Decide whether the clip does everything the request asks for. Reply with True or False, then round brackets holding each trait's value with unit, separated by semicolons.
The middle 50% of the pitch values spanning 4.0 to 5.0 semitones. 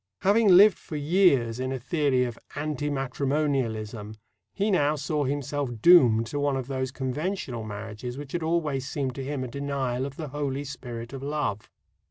False (3.0 semitones)